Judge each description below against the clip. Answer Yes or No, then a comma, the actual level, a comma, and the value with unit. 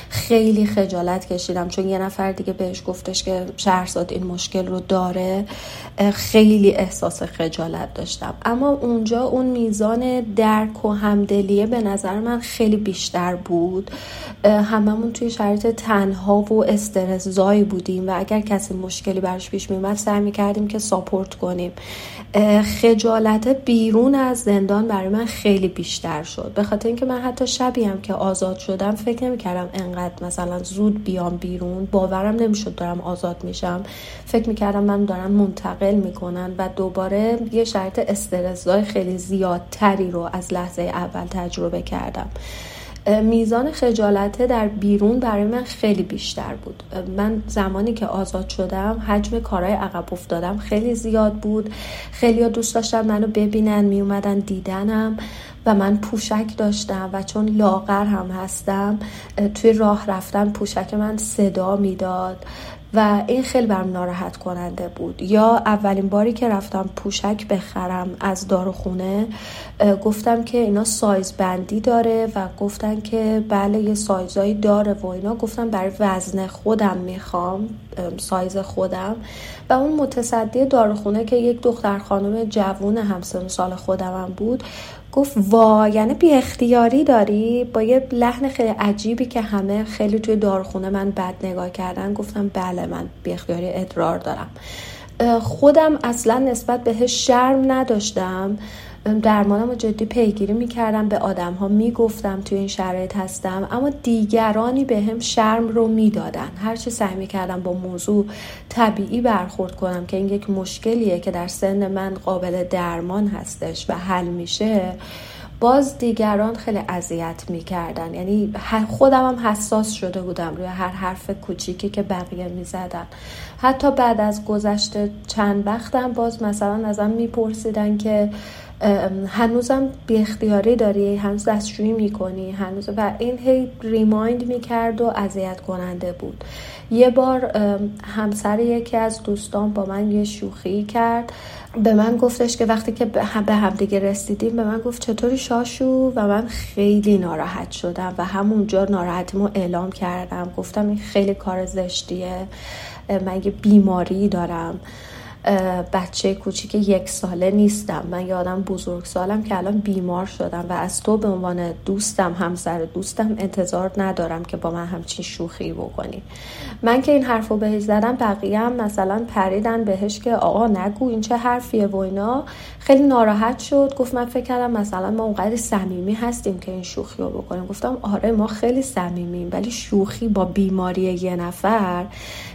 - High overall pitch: Yes, high, 205 Hz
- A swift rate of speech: No, average, 145 wpm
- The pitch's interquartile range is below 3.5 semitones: Yes, average, 3.0 semitones